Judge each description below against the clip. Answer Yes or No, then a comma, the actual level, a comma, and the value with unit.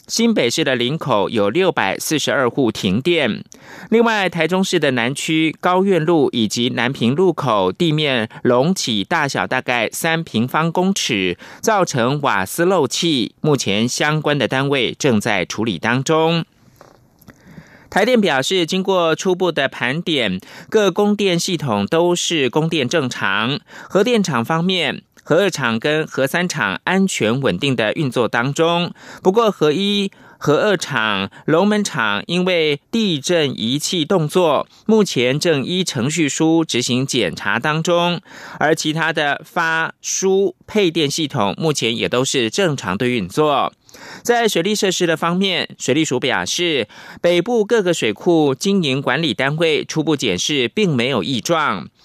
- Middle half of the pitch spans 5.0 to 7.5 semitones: Yes, wide, 5.6 semitones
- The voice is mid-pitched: Yes, medium, 160 Hz